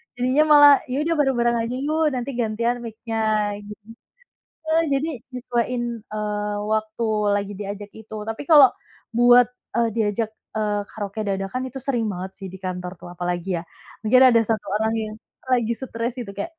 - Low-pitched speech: No, high, 225 Hz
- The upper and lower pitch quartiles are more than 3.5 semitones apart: No, average, 3.2 semitones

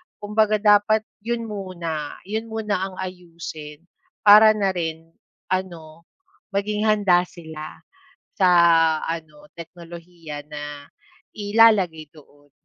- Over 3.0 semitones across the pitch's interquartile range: Yes, average, 4.5 semitones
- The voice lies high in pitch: No, medium, 180 Hz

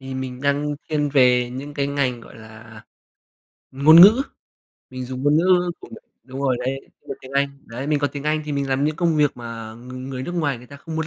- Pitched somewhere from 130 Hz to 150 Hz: Yes, medium, 140 Hz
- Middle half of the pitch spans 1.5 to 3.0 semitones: Yes, average, 2.7 semitones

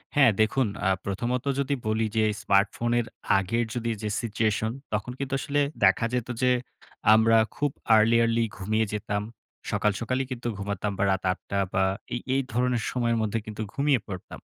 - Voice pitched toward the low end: Yes, low, 115 Hz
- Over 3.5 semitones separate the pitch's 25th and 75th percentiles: No, average, 2.9 semitones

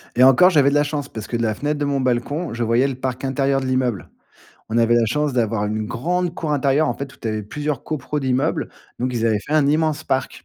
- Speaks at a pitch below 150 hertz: Yes, low, 135 Hz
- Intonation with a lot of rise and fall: No, average, 3.8 semitones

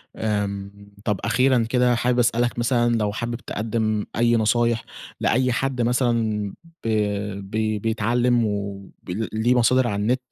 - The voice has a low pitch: Yes, low, 115 Hz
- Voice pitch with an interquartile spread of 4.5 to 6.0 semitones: No, narrow, 2.4 semitones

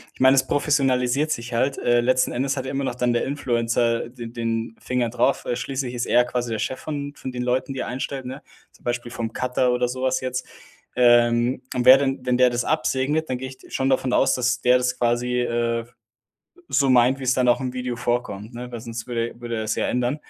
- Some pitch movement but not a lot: No, narrow, 1.6 semitones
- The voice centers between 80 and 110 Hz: No, low, 125 Hz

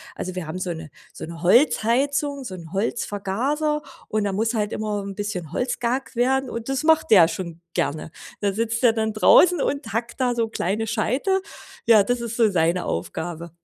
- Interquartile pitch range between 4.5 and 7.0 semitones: Yes, average, 4.9 semitones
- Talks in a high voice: Yes, high, 220 Hz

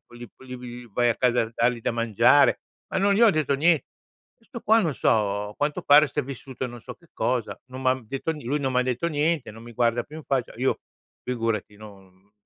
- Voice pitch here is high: No, low, 125 Hz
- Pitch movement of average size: Yes, average, 4.0 semitones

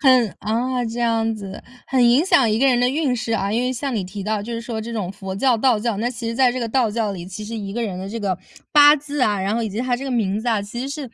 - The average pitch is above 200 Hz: Yes, high, 230 Hz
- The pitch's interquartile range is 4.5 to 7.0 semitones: No, average, 3.2 semitones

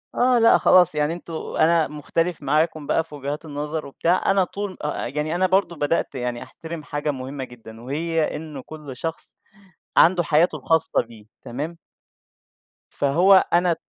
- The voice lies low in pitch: No, medium, 155 Hz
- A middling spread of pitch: Yes, average, 3.0 semitones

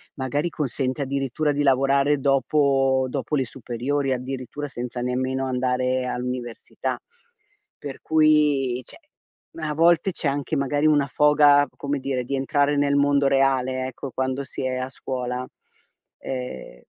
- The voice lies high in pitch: No, low, 135 Hz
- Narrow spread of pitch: Yes, narrow, 2.0 semitones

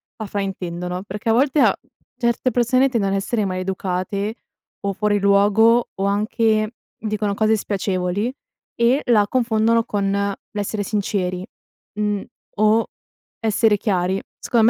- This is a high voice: Yes, high, 210 Hz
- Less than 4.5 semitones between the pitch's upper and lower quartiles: Yes, narrow, 2.4 semitones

